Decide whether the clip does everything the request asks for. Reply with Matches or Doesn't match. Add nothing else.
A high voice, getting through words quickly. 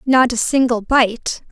Doesn't match